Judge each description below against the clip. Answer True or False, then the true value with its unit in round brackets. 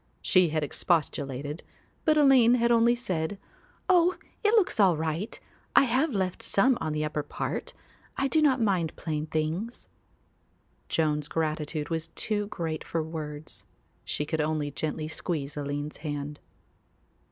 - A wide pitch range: True (7.1 semitones)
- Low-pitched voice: False (160 Hz)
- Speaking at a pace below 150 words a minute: True (140 wpm)